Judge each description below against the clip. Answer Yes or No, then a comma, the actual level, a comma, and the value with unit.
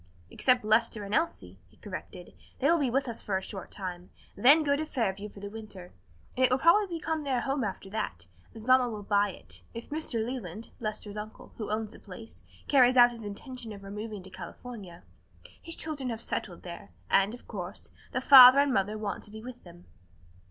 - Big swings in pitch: No, average, 4.4 semitones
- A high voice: Yes, high, 220 Hz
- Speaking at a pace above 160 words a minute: Yes, fast, 205 wpm